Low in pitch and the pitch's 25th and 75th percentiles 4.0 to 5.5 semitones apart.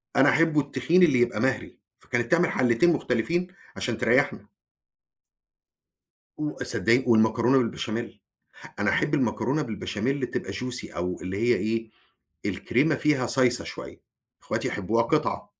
Yes: low, 125 Hz; average, 4.3 semitones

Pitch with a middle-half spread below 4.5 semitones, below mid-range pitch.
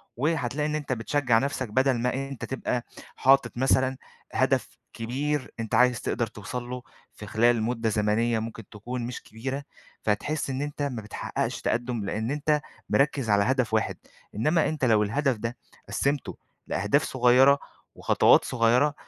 Yes: average, 3.5 semitones; low, 125 Hz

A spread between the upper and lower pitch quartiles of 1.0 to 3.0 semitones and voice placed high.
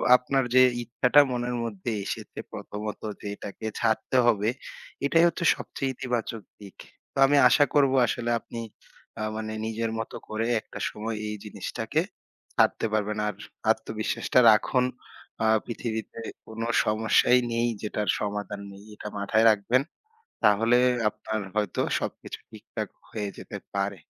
No: narrow, 2.4 semitones; low, 110 Hz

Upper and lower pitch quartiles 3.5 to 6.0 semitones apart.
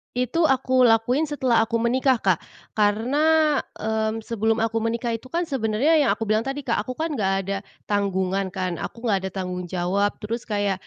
Yes: average, 4.1 semitones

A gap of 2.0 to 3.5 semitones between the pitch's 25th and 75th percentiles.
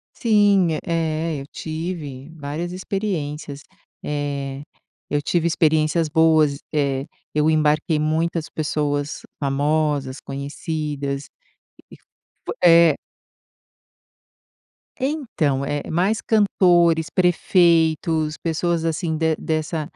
Yes: narrow, 2.5 semitones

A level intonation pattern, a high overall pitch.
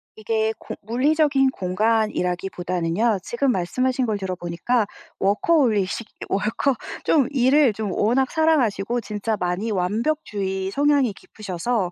No: average, 5.1 semitones; high, 220 Hz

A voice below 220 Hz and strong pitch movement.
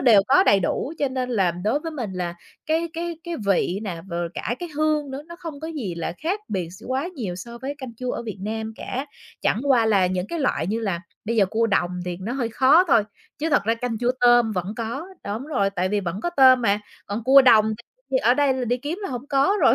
No: high, 240 Hz; wide, 5.7 semitones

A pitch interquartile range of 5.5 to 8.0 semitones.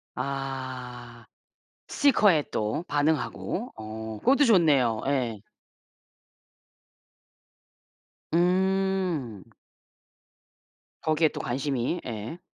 Yes: wide, 6.9 semitones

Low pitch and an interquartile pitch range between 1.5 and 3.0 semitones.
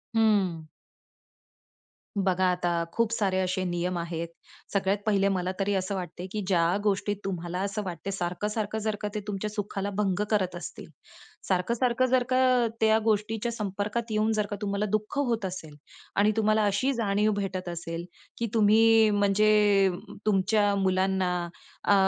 No: high, 200 Hz; narrow, 2.5 semitones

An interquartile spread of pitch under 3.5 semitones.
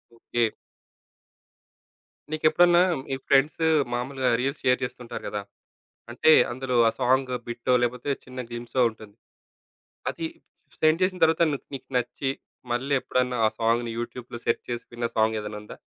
Yes: narrow, 2.5 semitones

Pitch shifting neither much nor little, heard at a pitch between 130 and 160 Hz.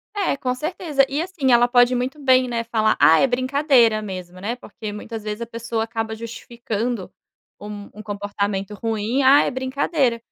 No: average, 3.4 semitones; high, 235 Hz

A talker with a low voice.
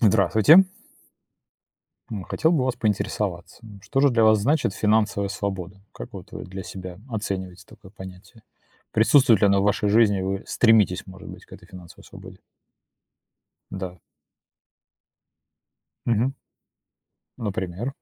Yes: low, 100 Hz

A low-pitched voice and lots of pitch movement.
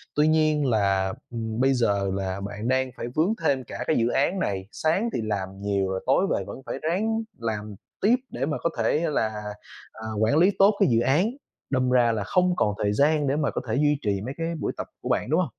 Yes: low, 130 Hz; wide, 6.9 semitones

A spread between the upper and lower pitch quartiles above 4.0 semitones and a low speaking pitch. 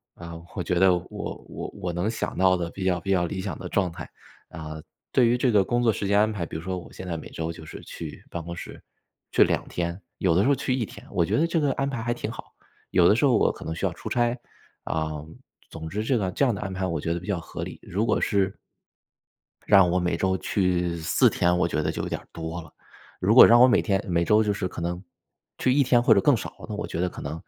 Yes: average, 4.6 semitones; very low, 95 Hz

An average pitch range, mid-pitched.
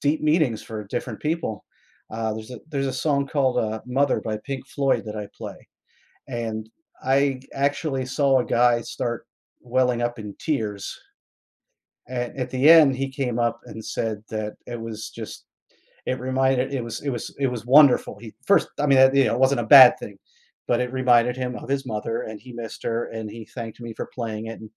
No: average, 3.1 semitones; low, 125 Hz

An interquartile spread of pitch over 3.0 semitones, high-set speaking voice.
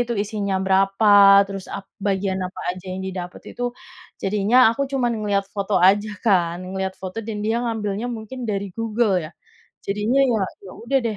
No: average, 2.7 semitones; high, 205 Hz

